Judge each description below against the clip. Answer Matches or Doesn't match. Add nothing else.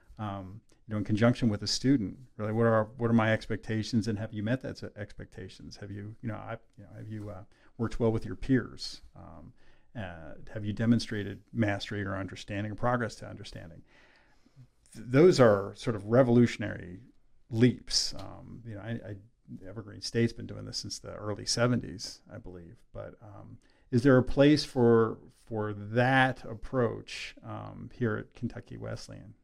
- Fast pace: Doesn't match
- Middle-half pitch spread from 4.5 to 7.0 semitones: Doesn't match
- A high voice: Doesn't match